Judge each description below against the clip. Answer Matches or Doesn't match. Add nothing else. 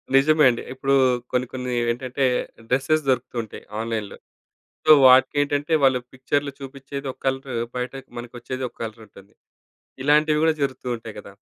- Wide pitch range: Doesn't match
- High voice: Doesn't match